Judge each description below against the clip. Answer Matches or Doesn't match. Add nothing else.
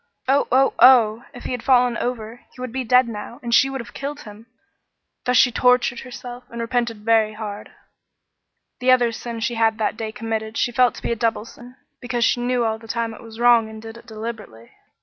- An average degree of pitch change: Doesn't match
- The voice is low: Doesn't match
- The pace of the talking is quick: Matches